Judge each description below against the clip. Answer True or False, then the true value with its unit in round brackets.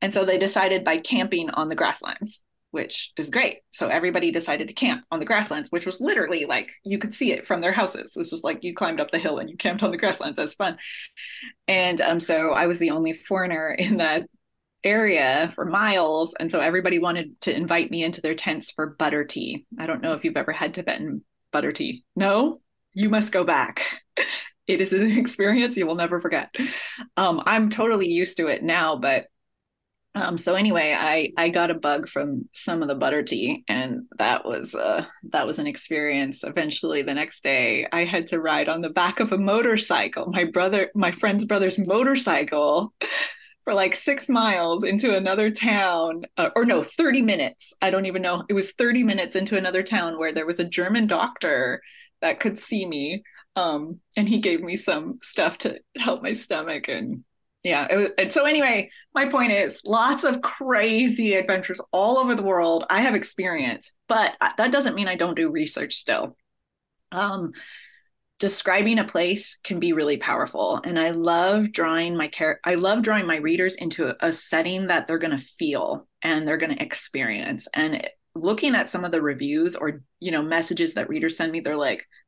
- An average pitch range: False (6.1 semitones)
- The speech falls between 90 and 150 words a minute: False (195 wpm)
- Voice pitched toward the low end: False (190 Hz)